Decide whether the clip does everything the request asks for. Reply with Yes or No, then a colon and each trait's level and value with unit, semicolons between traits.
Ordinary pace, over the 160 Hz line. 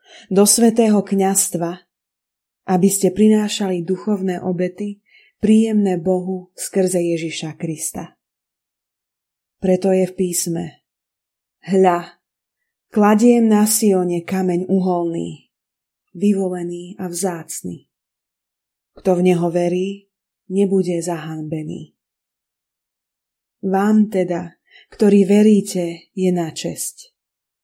No: slow, 85 wpm; medium, 185 Hz